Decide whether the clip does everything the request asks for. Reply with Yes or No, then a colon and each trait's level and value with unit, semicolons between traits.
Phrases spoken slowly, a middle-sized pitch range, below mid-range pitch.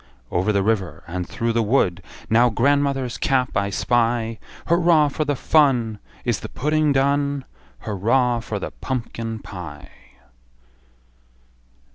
Yes: slow, 125 wpm; average, 4.7 semitones; low, 120 Hz